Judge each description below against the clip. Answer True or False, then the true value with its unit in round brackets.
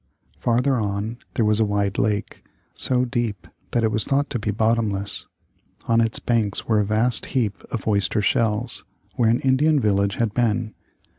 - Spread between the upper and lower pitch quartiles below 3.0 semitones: True (2.5 semitones)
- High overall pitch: False (110 Hz)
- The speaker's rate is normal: True (170 wpm)